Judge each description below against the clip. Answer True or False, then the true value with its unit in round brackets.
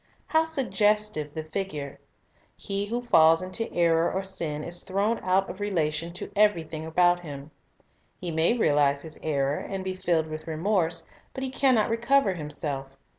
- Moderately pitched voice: True (175 Hz)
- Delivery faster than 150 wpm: True (165 wpm)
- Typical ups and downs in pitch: True (4.8 semitones)